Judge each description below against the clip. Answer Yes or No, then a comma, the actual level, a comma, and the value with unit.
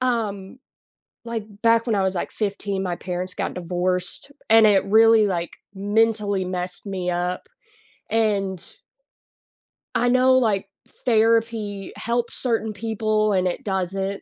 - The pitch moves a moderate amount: Yes, average, 3.1 semitones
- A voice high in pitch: Yes, high, 205 Hz